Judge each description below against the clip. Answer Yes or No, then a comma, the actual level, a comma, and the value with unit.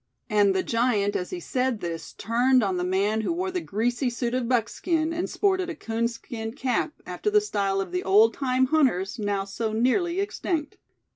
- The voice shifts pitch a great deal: Yes, wide, 6.6 semitones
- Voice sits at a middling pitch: No, high, 235 Hz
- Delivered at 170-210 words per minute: Yes, average, 190 wpm